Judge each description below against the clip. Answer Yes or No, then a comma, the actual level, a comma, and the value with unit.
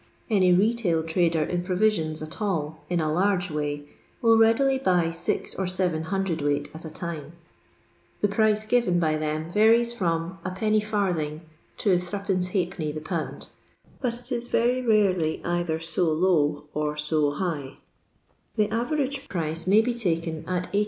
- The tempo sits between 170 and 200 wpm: No, average, 150 wpm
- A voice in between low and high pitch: Yes, medium, 180 Hz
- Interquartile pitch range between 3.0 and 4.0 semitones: No, average, 5.1 semitones